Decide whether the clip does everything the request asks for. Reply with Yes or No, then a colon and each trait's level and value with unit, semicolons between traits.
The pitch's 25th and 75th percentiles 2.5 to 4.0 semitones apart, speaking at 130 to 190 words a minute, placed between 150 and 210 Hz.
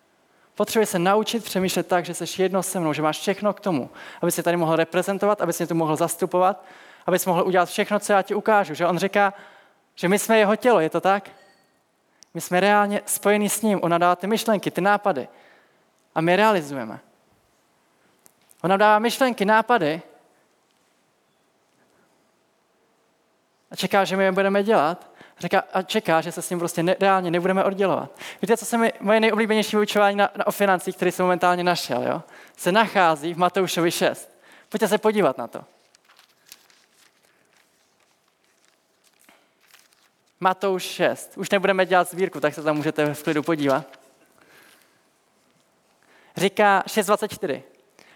Yes: average, 2.9 semitones; average, 155 wpm; high, 190 Hz